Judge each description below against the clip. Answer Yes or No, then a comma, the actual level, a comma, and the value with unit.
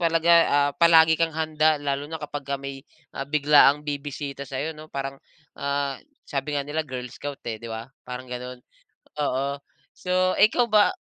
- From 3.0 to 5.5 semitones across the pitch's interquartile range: No, narrow, 2.4 semitones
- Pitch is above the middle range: No, medium, 145 Hz